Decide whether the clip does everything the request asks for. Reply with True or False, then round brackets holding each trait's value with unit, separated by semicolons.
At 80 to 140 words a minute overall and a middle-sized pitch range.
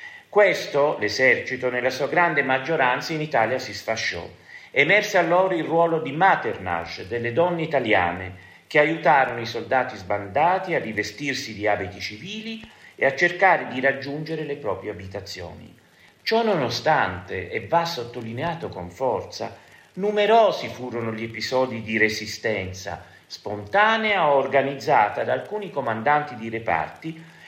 False (125 wpm; 7.1 semitones)